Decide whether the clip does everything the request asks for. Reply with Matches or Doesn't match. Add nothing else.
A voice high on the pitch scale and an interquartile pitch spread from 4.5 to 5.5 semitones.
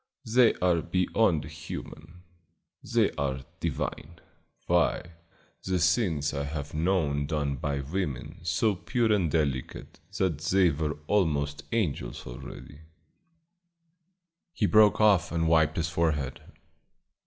Doesn't match